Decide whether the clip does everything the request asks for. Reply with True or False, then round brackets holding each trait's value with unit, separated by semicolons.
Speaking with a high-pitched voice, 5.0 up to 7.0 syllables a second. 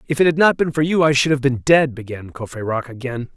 False (135 Hz; 5.9 syllables/s)